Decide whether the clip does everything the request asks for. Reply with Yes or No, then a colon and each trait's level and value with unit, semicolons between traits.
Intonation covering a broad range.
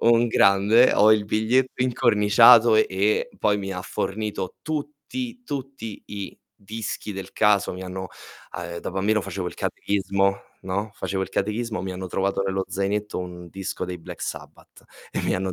No: average, 2.9 semitones